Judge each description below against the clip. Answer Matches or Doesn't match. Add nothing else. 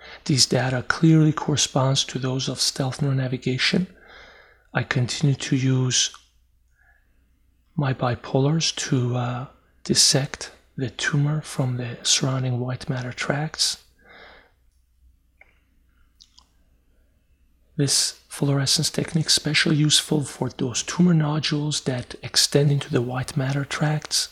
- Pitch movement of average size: Doesn't match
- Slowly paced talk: Matches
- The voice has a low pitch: Matches